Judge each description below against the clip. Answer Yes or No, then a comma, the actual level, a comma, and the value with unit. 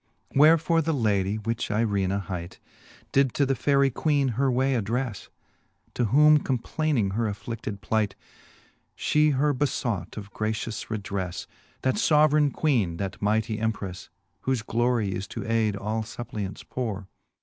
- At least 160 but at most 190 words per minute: No, average, 140 wpm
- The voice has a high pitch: No, low, 115 Hz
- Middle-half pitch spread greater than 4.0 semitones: Yes, average, 5.0 semitones